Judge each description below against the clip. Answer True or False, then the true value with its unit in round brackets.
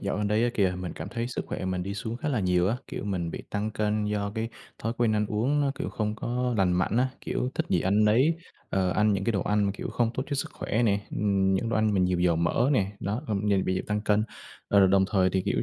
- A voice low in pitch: True (105 Hz)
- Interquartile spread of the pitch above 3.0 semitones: False (2.7 semitones)